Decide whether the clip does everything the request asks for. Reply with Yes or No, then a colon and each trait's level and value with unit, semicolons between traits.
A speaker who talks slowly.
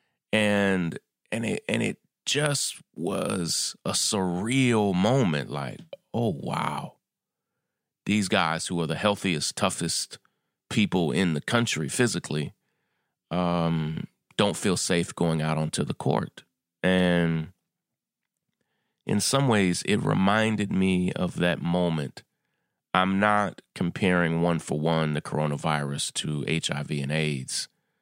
Yes: slow, 120 wpm